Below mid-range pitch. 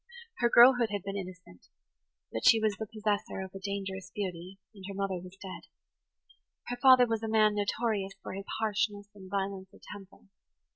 No: high, 200 Hz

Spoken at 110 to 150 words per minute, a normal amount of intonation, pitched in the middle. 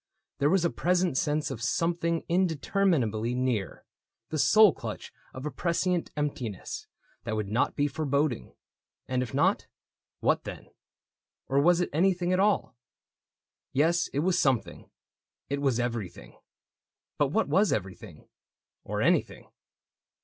No: average, 145 wpm; wide, 5.9 semitones; medium, 145 Hz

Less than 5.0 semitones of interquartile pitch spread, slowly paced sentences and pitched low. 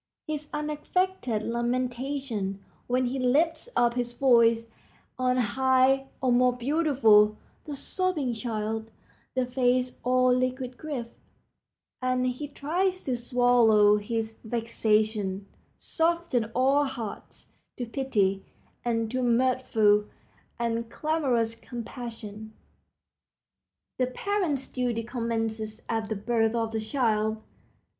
No: average, 3.0 semitones; slow, 105 wpm; high, 245 Hz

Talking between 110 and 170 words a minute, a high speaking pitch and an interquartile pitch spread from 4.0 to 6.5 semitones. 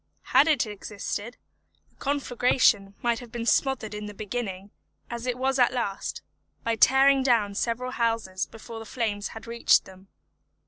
No: average, 155 wpm; high, 230 Hz; average, 3.2 semitones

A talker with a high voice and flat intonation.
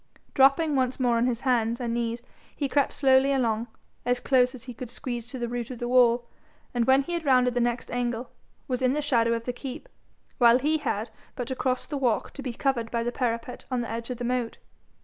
Yes: high, 245 Hz; narrow, 1.8 semitones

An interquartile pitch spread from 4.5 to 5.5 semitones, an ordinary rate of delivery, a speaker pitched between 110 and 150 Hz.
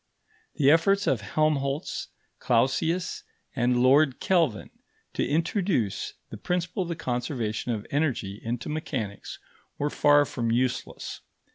No: average, 4.9 semitones; slow, 120 wpm; medium, 140 Hz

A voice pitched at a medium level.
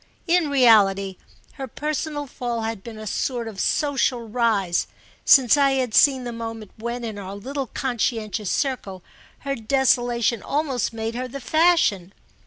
No: high, 240 Hz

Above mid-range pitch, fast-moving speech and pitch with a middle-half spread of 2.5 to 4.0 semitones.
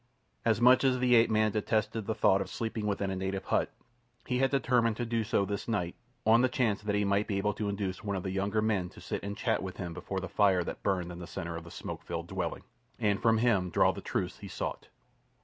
No: low, 105 Hz; fast, 255 wpm; average, 2.8 semitones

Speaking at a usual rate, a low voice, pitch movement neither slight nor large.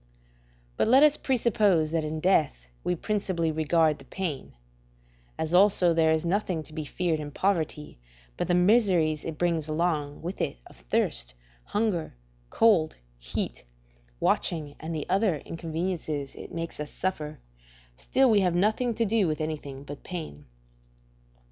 No: average, 150 wpm; medium, 165 Hz; average, 3.8 semitones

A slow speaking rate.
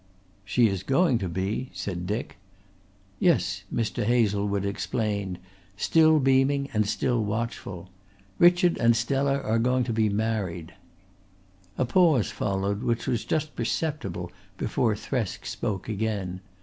Yes: slow, 125 wpm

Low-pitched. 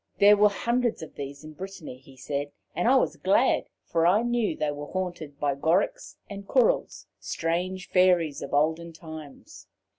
No: medium, 170 Hz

